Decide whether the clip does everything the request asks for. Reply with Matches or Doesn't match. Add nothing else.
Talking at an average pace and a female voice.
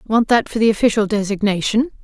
Matches